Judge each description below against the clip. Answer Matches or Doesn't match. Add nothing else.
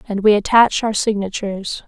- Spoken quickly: Doesn't match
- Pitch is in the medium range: Doesn't match